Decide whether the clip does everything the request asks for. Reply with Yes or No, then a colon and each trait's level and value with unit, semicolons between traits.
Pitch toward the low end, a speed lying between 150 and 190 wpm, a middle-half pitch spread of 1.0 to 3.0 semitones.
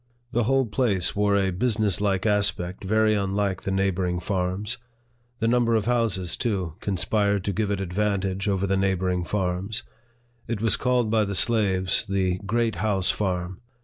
Yes: low, 100 Hz; average, 160 wpm; narrow, 2.6 semitones